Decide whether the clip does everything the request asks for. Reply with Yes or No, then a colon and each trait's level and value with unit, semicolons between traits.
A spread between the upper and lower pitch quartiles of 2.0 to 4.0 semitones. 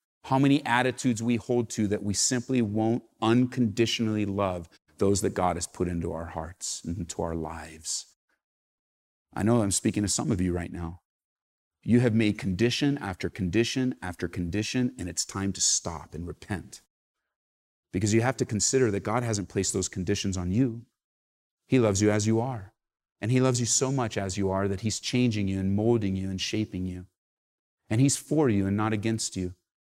No: average, 4.5 semitones